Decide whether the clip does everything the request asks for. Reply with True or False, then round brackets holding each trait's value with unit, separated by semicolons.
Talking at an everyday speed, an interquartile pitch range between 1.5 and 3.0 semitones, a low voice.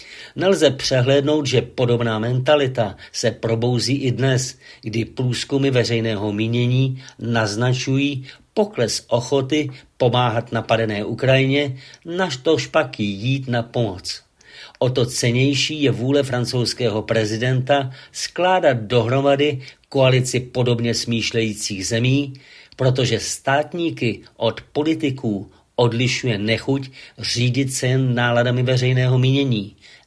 False (100 wpm; 2.7 semitones; 125 Hz)